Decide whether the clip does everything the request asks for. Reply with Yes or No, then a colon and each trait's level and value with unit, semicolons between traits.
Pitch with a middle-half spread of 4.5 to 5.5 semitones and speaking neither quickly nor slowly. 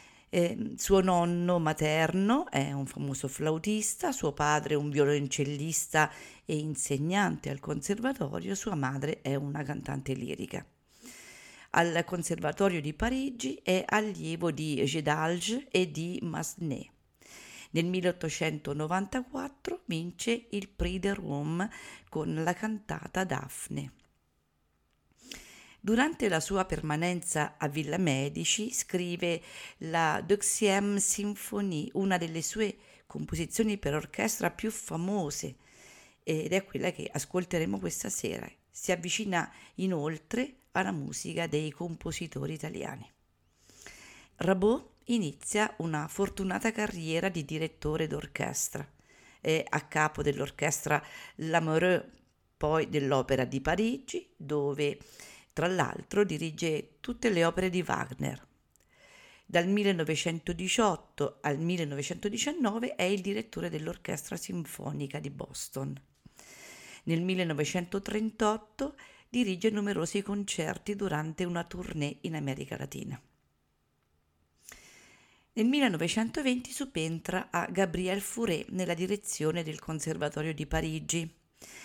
No: average, 5.1 semitones; slow, 100 wpm